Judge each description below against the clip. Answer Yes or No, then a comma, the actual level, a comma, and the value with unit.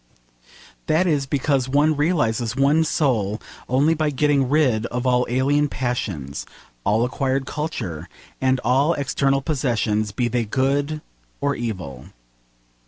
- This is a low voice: Yes, low, 130 Hz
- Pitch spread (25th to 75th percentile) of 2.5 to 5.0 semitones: Yes, average, 3.7 semitones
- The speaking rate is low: Yes, slow, 125 wpm